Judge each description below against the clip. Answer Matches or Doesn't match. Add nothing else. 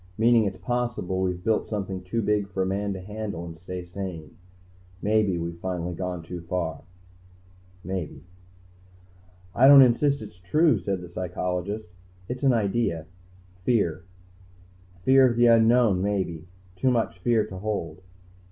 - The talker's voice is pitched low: Matches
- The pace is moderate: Matches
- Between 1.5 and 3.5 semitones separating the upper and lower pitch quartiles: Doesn't match